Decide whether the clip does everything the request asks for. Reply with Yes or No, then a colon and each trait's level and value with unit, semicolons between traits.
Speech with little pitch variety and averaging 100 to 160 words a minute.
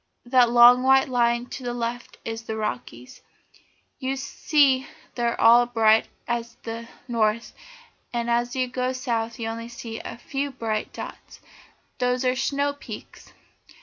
Yes: narrow, 1.9 semitones; average, 150 wpm